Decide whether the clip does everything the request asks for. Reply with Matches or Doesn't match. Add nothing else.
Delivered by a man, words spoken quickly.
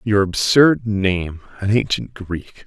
Doesn't match